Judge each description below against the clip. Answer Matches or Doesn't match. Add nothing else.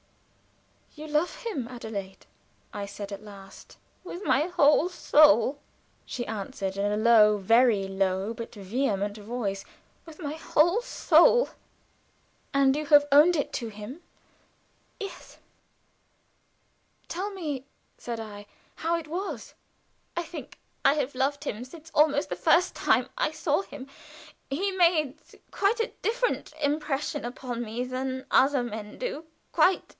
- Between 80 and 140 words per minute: Matches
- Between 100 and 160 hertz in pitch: Doesn't match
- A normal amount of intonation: Doesn't match